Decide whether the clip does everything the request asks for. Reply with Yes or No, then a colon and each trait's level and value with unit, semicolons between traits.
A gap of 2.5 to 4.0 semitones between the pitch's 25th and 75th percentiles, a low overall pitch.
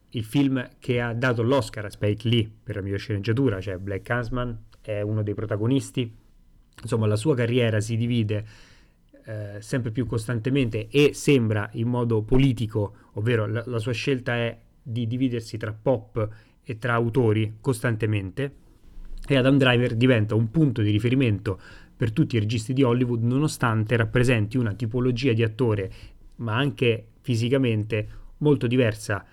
Yes: average, 2.9 semitones; low, 120 Hz